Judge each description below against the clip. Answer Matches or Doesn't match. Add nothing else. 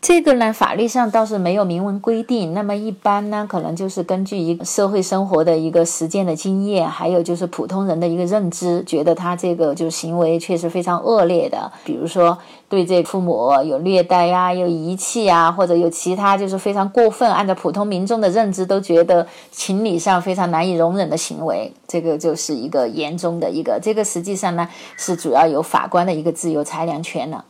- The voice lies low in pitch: Doesn't match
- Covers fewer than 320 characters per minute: Doesn't match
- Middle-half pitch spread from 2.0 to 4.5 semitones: Matches